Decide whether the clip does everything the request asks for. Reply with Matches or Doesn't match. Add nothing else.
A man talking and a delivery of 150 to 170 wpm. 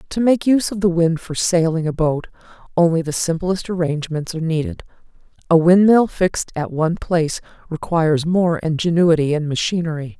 Doesn't match